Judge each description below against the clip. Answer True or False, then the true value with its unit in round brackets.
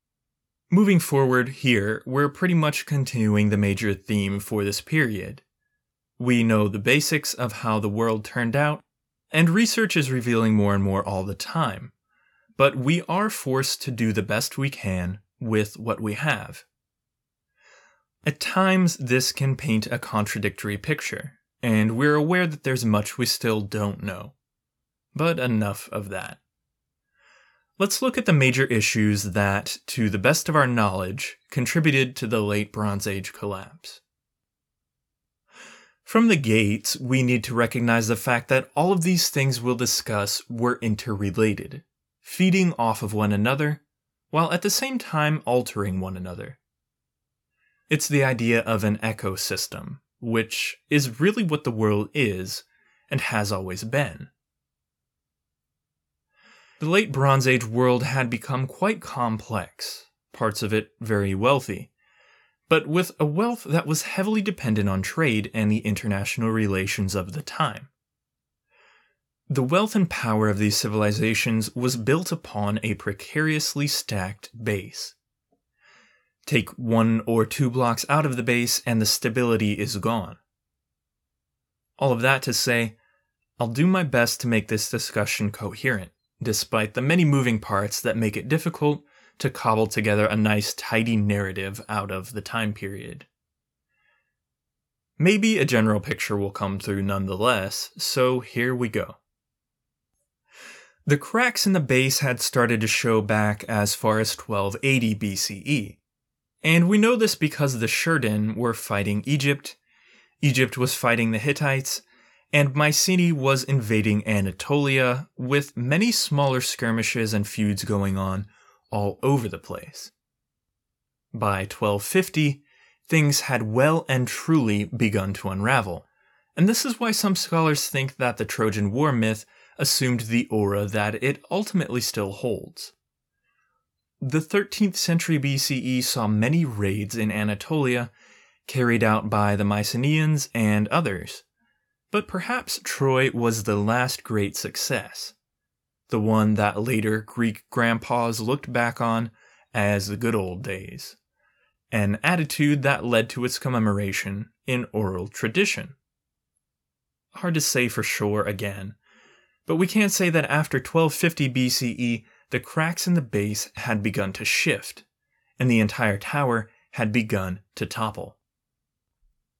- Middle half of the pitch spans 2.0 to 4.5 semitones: False (5.3 semitones)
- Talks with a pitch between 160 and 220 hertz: False (120 Hz)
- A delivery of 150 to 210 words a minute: False (140 wpm)